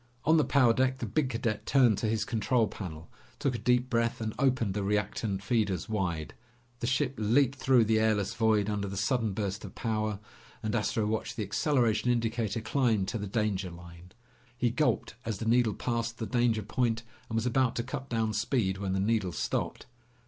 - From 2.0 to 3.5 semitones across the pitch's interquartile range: Yes, average, 2.9 semitones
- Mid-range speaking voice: No, low, 110 Hz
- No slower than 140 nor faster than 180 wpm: No, average, 195 wpm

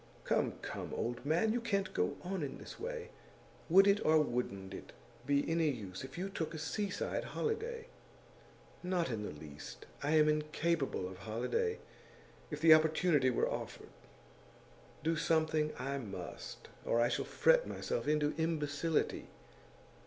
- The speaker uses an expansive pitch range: Yes, wide, 5.8 semitones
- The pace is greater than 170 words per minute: No, average, 145 wpm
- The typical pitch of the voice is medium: Yes, medium, 155 Hz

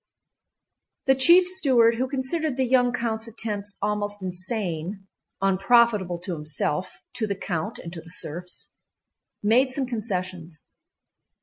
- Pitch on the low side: No, high, 210 Hz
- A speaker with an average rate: No, slow, 115 wpm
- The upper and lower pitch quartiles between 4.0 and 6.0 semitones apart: Yes, average, 5.2 semitones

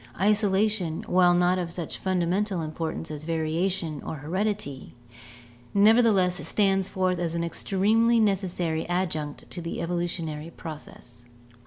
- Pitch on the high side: No, medium, 175 Hz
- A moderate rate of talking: No, slow, 120 wpm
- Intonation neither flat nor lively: Yes, average, 3.1 semitones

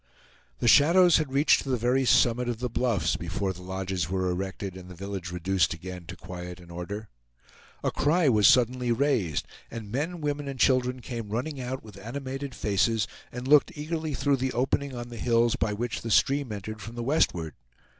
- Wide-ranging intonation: Yes, wide, 5.8 semitones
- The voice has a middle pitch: No, low, 120 Hz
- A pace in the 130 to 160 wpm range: No, average, 195 wpm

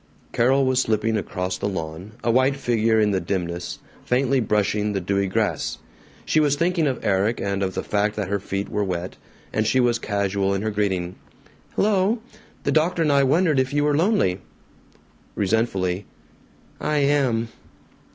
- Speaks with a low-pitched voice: Yes, low, 110 Hz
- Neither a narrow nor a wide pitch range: No, wide, 5.7 semitones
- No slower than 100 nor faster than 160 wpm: No, average, 170 wpm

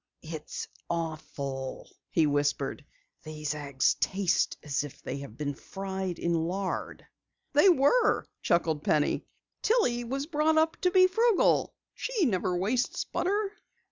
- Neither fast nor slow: No, slow, 130 wpm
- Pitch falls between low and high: Yes, medium, 180 Hz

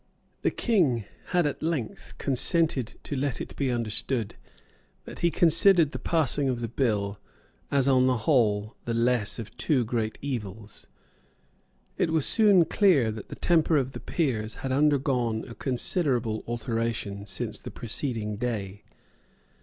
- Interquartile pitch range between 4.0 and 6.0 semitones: Yes, average, 4.8 semitones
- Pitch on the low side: Yes, low, 125 Hz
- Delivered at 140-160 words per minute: Yes, average, 145 wpm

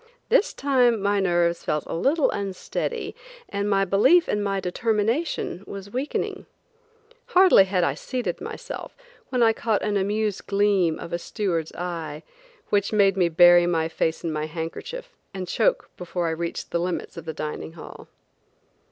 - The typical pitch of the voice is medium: No, high, 195 Hz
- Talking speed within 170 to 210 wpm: No, average, 160 wpm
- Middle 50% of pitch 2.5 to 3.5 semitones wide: No, average, 4.3 semitones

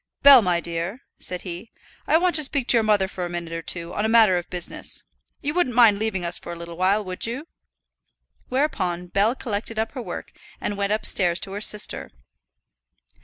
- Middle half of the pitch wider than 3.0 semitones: Yes, average, 4.8 semitones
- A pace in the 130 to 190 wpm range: No, fast, 205 wpm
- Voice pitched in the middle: No, high, 205 Hz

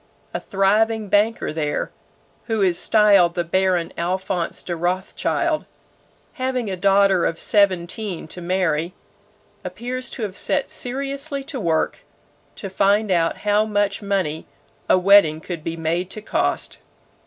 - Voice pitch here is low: No, high, 195 Hz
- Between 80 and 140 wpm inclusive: Yes, slow, 135 wpm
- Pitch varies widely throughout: No, average, 3.7 semitones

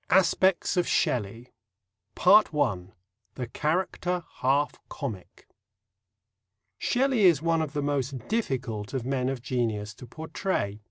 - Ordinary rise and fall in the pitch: No, wide, 6.0 semitones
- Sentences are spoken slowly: Yes, slow, 120 wpm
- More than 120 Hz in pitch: Yes, low, 135 Hz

